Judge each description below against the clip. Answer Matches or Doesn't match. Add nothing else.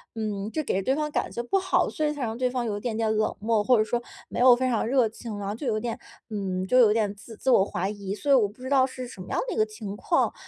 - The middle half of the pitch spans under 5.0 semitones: Matches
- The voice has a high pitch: Matches